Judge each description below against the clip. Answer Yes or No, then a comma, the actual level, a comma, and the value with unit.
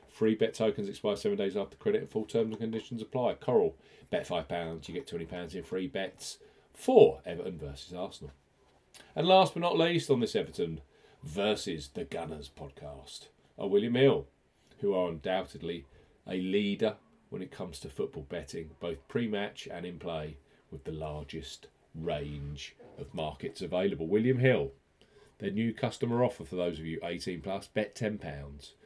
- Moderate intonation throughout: No, wide, 7.5 semitones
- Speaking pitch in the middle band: No, low, 105 Hz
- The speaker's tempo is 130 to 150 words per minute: No, average, 165 wpm